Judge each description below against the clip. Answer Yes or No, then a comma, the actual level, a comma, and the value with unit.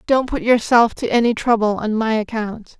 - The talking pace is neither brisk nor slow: Yes, average, 195 wpm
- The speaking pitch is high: Yes, high, 225 Hz